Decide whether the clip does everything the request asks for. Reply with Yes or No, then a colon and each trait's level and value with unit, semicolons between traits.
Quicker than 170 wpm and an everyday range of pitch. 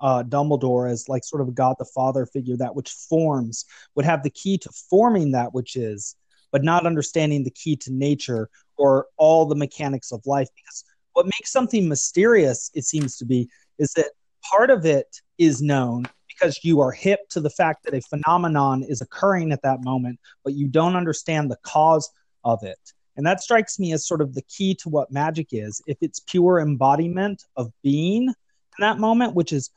Yes: average, 200 wpm; average, 4.3 semitones